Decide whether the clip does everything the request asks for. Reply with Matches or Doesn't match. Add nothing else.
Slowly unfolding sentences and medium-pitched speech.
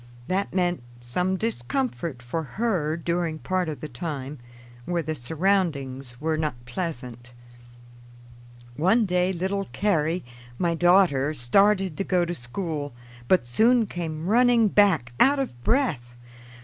Matches